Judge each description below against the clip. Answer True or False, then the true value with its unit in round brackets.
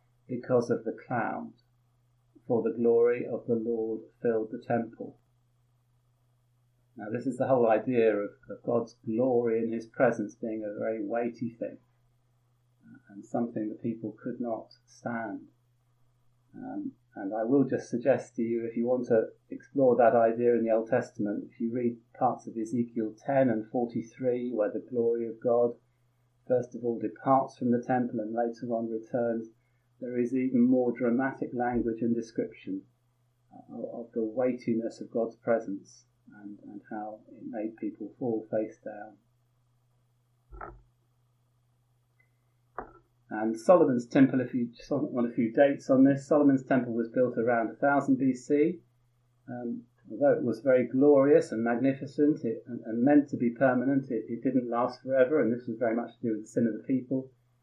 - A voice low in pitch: True (120 Hz)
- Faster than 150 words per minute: True (165 wpm)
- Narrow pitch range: True (1.3 semitones)